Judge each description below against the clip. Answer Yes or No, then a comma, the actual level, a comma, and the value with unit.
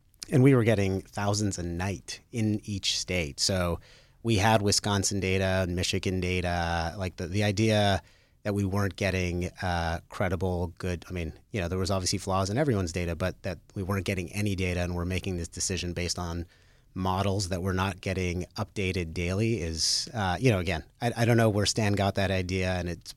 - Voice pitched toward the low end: Yes, very low, 95 Hz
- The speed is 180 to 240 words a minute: Yes, average, 200 wpm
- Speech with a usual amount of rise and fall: No, narrow, 2.3 semitones